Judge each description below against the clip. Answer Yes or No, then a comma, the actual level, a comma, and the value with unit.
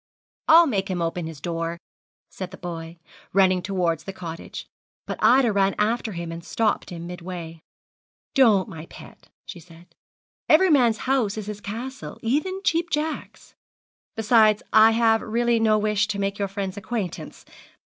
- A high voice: Yes, high, 200 Hz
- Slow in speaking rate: No, average, 160 wpm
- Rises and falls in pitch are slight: No, average, 4.6 semitones